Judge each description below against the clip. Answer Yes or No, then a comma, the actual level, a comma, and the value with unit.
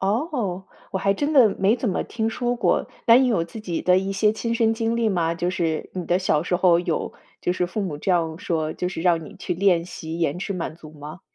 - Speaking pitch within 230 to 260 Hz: No, medium, 185 Hz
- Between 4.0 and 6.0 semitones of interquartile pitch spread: Yes, average, 4.7 semitones